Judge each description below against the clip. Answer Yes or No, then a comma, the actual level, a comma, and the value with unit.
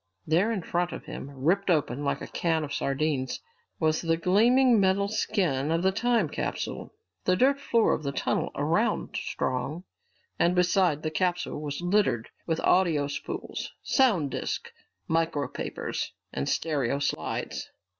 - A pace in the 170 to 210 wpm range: No, average, 145 wpm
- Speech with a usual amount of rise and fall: Yes, average, 4.9 semitones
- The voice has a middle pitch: Yes, medium, 165 Hz